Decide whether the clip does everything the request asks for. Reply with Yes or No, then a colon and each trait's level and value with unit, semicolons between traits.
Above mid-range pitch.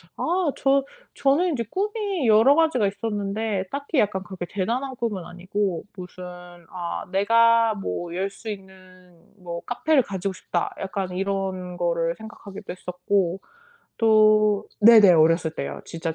Yes: high, 200 Hz